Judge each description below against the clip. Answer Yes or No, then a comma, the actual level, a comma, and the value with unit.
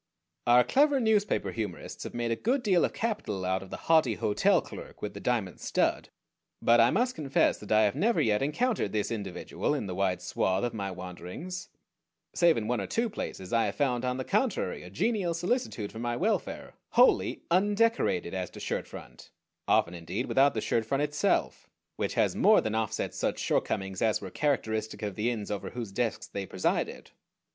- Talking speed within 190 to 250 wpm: Yes, average, 195 wpm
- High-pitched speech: No, low, 115 Hz